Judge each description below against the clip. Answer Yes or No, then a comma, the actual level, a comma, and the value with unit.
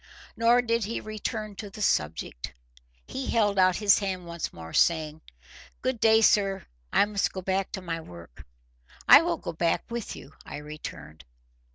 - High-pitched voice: Yes, high, 195 Hz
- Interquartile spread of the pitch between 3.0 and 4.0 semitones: No, average, 5.3 semitones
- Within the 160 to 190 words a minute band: Yes, average, 170 wpm